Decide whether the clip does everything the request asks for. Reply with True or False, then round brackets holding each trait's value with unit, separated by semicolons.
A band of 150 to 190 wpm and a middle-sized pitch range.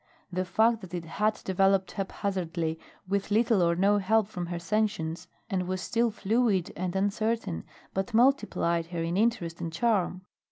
True (160 wpm; 3.8 semitones)